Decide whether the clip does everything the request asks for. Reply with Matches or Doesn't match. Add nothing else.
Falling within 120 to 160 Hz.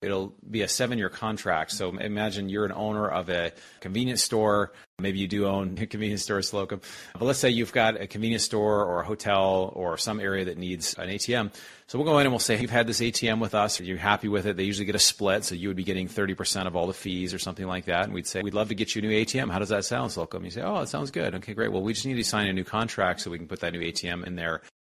Doesn't match